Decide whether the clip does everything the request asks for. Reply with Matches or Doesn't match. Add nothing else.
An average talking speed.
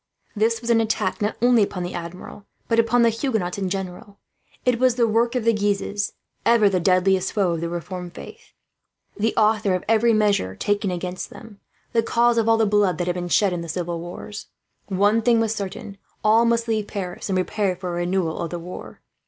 Doesn't match